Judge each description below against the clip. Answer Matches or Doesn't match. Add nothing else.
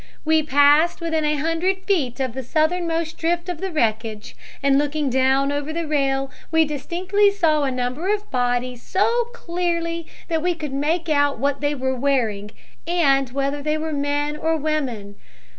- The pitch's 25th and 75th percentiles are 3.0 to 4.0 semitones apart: Matches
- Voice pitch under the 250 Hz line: Doesn't match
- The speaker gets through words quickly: Doesn't match